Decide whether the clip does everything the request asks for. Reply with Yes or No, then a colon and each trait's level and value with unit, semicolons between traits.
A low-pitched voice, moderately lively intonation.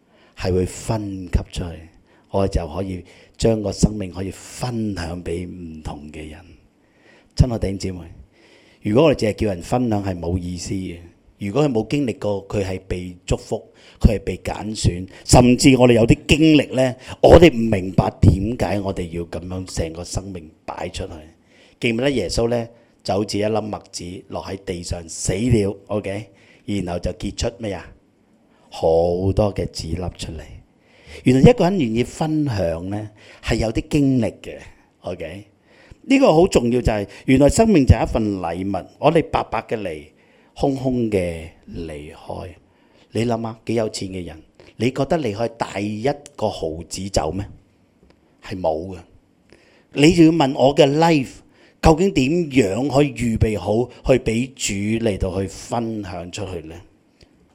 Yes: low, 100 Hz; average, 4.7 semitones